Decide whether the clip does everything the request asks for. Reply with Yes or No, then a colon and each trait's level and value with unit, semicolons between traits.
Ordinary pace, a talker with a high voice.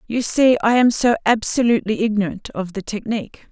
Yes: average, 170 wpm; high, 220 Hz